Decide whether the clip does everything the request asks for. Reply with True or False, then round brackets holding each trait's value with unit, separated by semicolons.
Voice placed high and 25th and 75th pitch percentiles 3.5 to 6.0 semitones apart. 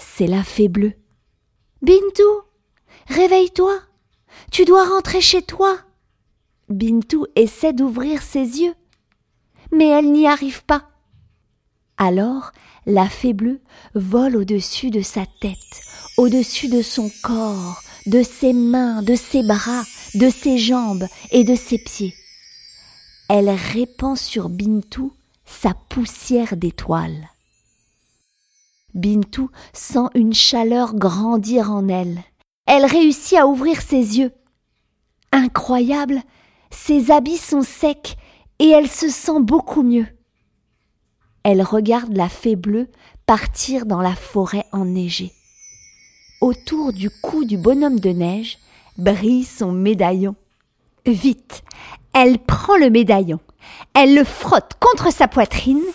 True (245 Hz; 5.6 semitones)